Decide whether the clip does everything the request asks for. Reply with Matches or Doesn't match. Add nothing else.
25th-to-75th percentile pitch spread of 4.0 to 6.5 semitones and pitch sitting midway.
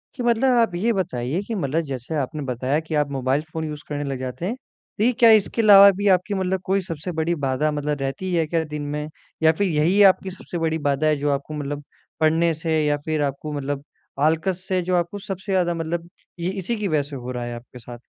Matches